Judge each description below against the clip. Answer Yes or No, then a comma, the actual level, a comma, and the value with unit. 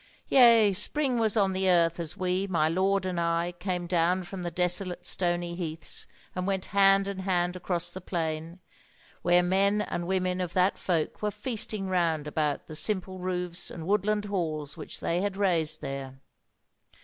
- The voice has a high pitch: No, medium, 180 Hz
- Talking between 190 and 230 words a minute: No, average, 175 wpm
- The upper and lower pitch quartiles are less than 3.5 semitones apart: Yes, narrow, 2.4 semitones